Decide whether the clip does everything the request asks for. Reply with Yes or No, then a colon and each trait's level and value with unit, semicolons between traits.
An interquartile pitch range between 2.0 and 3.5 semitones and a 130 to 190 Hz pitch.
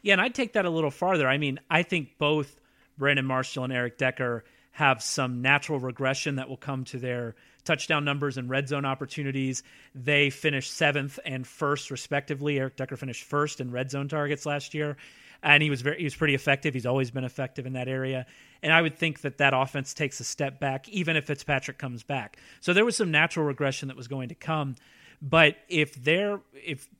Yes: narrow, 2.4 semitones; medium, 140 Hz